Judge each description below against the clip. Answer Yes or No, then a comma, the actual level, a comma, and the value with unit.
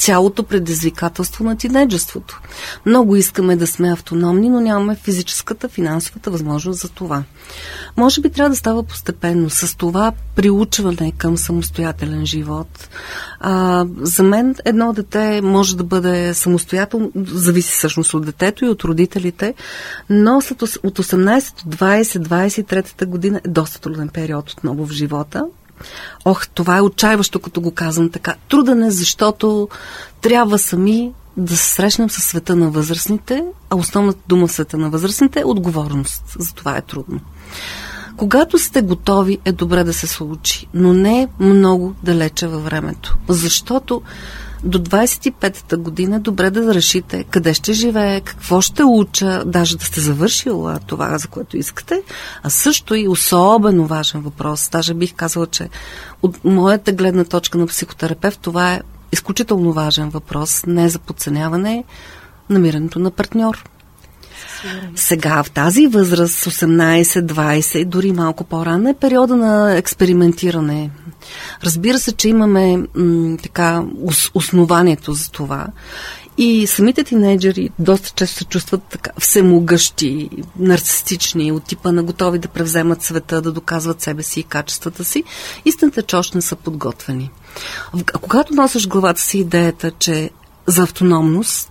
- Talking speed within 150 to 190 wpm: No, average, 140 wpm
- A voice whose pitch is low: No, medium, 180 Hz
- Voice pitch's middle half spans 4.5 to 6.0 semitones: No, average, 3.7 semitones